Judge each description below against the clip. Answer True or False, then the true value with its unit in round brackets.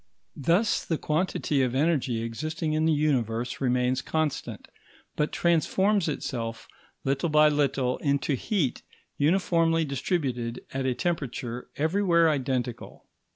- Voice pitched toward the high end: False (145 Hz)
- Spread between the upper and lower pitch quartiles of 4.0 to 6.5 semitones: True (4.3 semitones)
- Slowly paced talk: True (115 wpm)